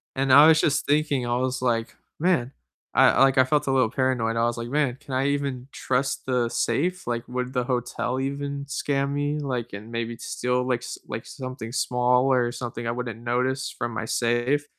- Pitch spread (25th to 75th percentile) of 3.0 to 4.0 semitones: No, narrow, 2.5 semitones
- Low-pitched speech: Yes, low, 125 Hz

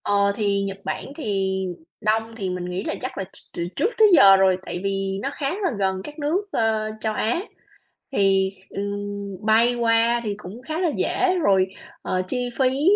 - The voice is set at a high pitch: Yes, high, 210 Hz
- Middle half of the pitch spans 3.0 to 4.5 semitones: Yes, average, 4.2 semitones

